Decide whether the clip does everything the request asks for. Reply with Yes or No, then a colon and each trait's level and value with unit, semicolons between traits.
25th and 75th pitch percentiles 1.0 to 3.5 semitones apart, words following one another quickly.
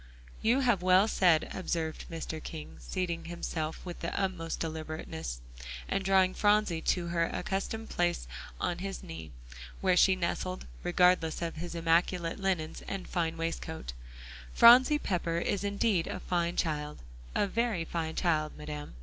No: average, 2.8 semitones; average, 145 wpm